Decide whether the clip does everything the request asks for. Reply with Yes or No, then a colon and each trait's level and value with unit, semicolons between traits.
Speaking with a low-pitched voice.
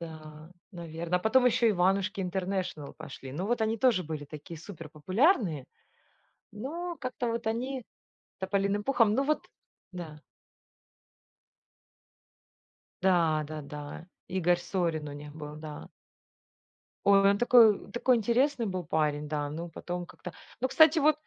No: medium, 185 Hz